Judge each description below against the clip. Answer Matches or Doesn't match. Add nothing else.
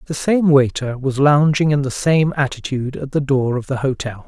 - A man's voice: Matches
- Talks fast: Matches